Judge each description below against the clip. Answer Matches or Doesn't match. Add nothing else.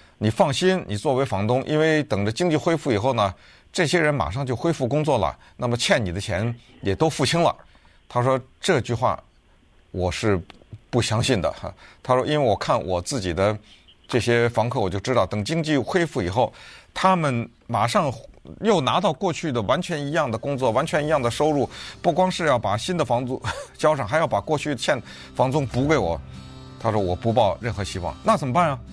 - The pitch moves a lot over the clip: Matches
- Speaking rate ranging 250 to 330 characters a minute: Matches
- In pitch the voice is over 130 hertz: Doesn't match